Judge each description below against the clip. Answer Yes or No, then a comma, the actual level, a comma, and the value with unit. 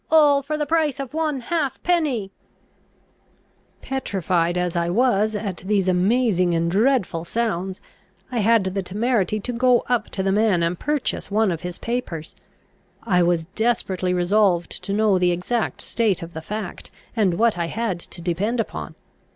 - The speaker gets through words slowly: No, average, 160 wpm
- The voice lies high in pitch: Yes, high, 205 Hz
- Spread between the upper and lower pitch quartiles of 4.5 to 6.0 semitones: Yes, average, 5.2 semitones